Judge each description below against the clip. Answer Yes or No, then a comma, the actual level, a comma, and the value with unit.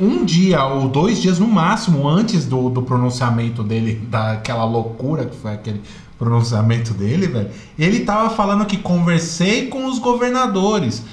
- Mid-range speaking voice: Yes, medium, 145 Hz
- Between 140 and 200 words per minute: Yes, average, 150 wpm